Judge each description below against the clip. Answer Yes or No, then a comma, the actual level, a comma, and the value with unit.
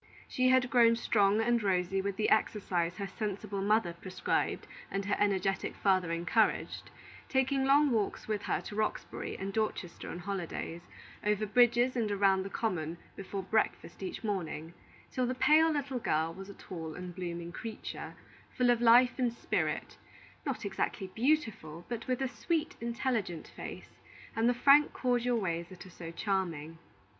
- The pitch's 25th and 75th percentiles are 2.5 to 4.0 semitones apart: No, average, 4.7 semitones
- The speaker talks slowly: No, average, 160 wpm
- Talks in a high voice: Yes, high, 205 Hz